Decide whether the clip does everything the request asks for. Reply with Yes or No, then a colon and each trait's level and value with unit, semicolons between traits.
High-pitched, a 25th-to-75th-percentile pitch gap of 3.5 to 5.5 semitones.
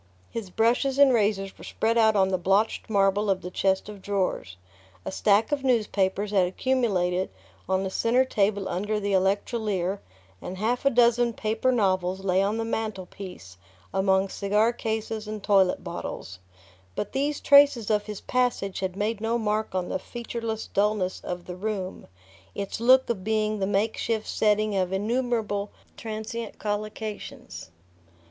No: high, 210 Hz; average, 2.9 semitones